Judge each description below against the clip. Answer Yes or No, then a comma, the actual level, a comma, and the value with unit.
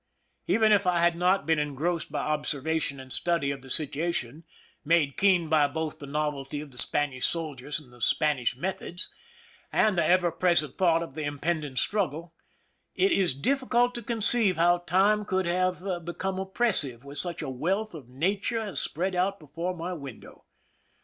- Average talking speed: Yes, average, 170 wpm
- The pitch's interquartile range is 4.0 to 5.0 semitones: Yes, average, 4.3 semitones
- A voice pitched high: No, medium, 170 Hz